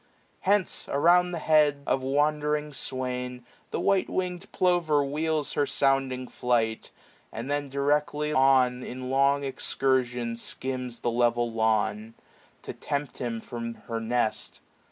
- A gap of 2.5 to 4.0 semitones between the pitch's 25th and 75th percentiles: Yes, average, 3.4 semitones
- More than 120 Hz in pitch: Yes, low, 135 Hz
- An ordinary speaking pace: No, slow, 130 wpm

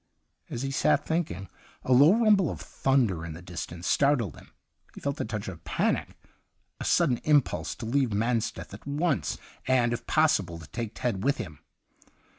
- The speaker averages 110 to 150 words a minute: No, average, 185 wpm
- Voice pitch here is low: Yes, low, 120 Hz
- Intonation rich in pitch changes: Yes, wide, 6.9 semitones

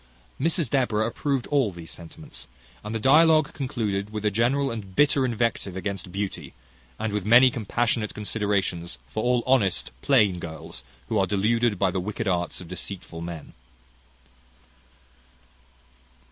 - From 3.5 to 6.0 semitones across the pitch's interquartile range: Yes, average, 4.3 semitones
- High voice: No, low, 105 Hz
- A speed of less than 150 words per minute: Yes, average, 140 wpm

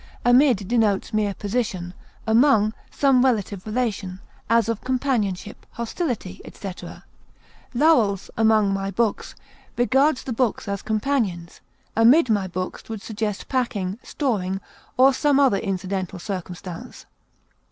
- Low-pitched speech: No, high, 215 Hz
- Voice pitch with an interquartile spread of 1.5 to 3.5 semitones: No, average, 4.4 semitones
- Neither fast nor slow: No, slow, 115 wpm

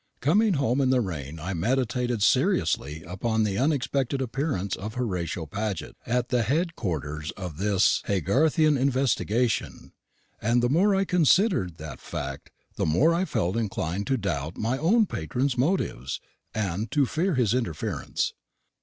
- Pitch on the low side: Yes, low, 115 Hz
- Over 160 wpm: No, average, 145 wpm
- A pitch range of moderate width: No, wide, 7.1 semitones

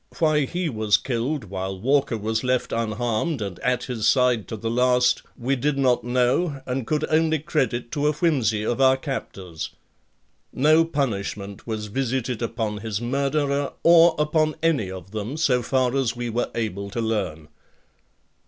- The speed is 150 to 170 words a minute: Yes, average, 160 wpm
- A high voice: No, low, 125 Hz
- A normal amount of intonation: Yes, average, 4.6 semitones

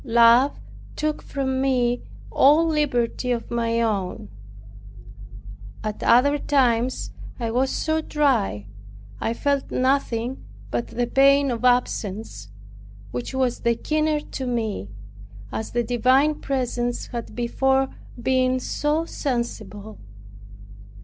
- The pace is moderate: No, slow, 110 wpm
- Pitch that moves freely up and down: No, average, 2.9 semitones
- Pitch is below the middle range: No, very high, 250 Hz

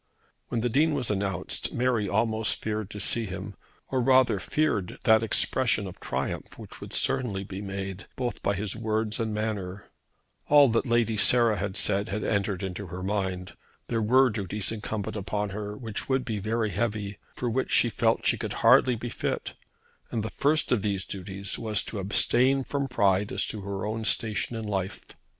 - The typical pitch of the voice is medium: No, low, 105 Hz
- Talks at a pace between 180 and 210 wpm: Yes, average, 185 wpm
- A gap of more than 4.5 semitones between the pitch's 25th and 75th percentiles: No, average, 3.0 semitones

